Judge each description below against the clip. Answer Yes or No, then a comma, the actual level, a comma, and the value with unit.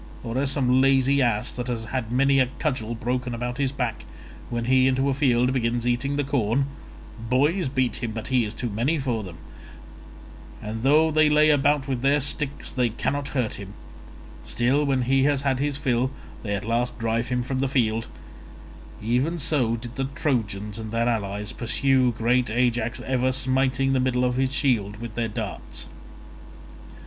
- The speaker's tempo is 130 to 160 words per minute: No, average, 175 wpm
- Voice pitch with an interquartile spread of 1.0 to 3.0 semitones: Yes, average, 2.7 semitones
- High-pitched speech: No, low, 125 Hz